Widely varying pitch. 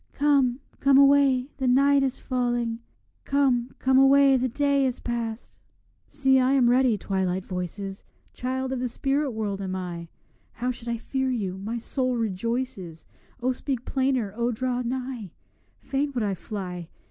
No: average, 3.5 semitones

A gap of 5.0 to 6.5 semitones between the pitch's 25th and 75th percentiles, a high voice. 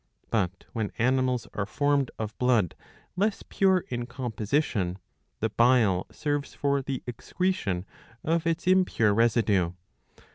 No: wide, 5.4 semitones; low, 125 Hz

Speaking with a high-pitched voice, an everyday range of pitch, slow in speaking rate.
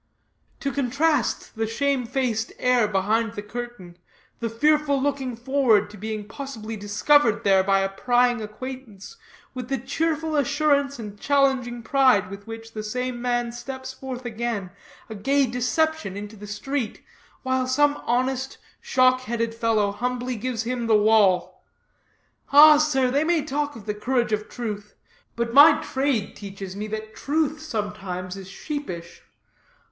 No: high, 240 Hz; average, 4.3 semitones; average, 145 wpm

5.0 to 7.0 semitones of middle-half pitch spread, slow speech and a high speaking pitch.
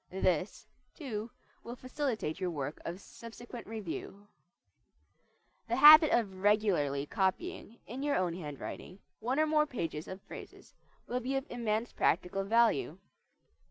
Yes: average, 5.3 semitones; slow, 130 wpm; high, 215 Hz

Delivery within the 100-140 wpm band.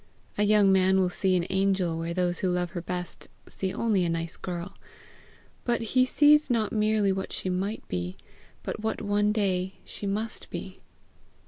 No: average, 180 wpm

